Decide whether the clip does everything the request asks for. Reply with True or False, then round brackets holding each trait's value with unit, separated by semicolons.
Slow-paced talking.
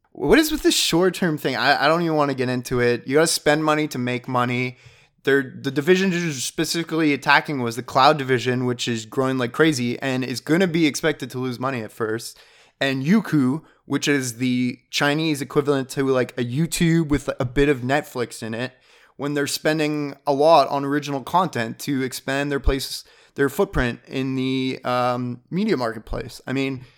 False (200 wpm)